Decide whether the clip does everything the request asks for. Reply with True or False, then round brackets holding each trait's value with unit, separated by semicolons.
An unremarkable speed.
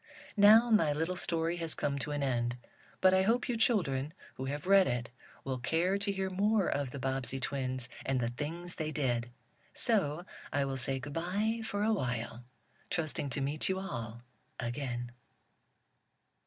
True (170 wpm)